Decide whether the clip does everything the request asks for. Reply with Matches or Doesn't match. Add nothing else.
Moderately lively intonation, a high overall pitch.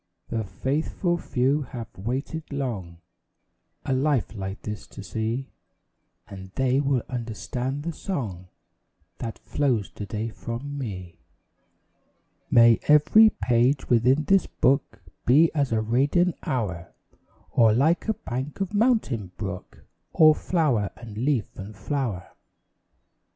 Doesn't match